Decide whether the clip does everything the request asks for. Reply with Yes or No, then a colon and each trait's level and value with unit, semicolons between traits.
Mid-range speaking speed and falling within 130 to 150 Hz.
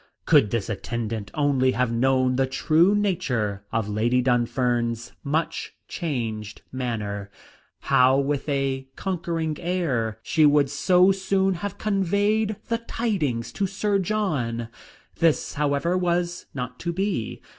No: slow, 125 wpm; medium, 140 Hz